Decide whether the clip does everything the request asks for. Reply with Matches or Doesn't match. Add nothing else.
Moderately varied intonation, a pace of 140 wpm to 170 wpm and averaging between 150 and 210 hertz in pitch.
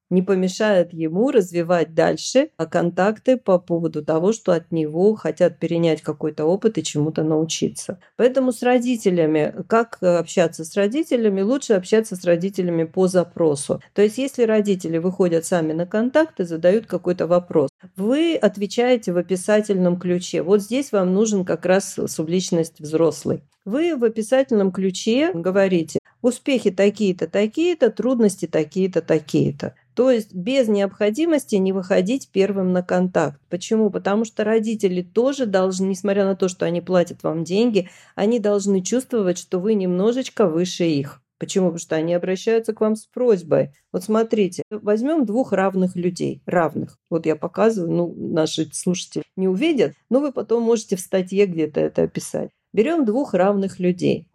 Matches